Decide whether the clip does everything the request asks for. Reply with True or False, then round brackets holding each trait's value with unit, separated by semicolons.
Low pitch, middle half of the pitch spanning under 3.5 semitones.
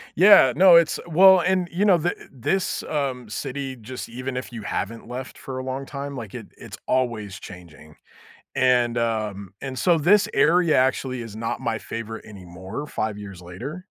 False (130 Hz; 5.5 semitones)